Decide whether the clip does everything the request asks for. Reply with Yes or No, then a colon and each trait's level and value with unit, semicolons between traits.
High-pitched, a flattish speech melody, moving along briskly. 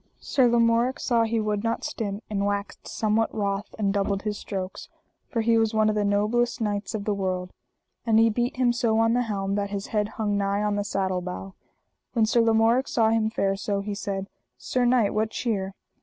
Yes: high, 215 Hz; narrow, 2.2 semitones; fast, 210 wpm